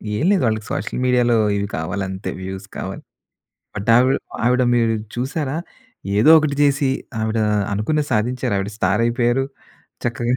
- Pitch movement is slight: No, average, 4.0 semitones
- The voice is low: Yes, low, 120 Hz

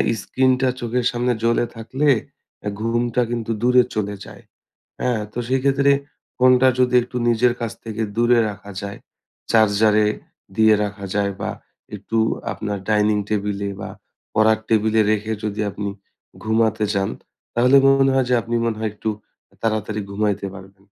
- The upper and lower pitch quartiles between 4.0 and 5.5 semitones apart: No, average, 2.8 semitones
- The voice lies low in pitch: Yes, low, 110 Hz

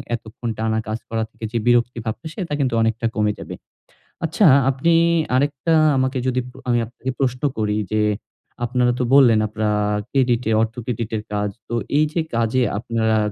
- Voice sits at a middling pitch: No, low, 120 Hz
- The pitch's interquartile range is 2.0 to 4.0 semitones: Yes, average, 2.9 semitones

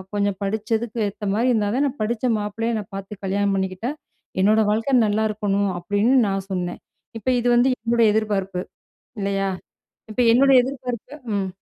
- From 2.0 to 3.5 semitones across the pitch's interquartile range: Yes, average, 3.1 semitones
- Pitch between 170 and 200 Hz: No, high, 210 Hz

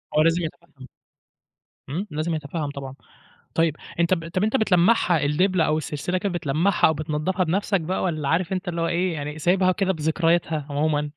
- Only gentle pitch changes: No, average, 3.3 semitones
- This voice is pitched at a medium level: Yes, medium, 165 Hz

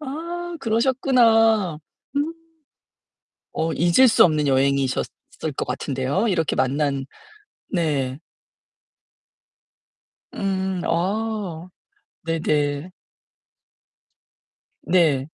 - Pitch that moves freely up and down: Yes, wide, 7.6 semitones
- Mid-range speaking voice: Yes, medium, 175 Hz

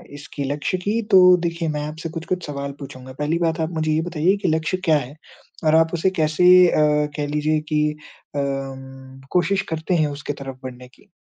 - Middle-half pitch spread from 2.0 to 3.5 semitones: Yes, average, 2.8 semitones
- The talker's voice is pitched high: No, medium, 155 Hz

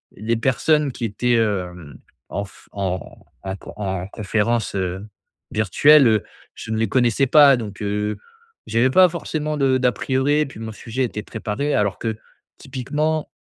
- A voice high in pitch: No, low, 115 Hz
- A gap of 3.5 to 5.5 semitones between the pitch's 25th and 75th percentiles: Yes, average, 4.7 semitones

